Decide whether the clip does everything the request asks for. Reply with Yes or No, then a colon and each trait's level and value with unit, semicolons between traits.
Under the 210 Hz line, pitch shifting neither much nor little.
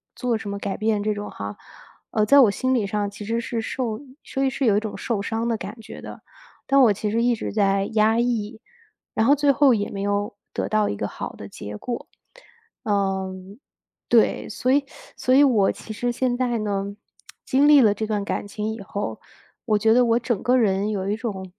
No: high, 215 Hz; average, 3.0 semitones